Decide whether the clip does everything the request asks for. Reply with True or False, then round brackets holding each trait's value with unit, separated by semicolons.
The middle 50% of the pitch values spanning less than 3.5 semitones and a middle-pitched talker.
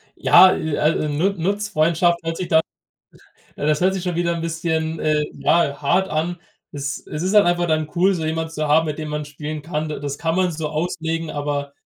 True (2.4 semitones; 160 Hz)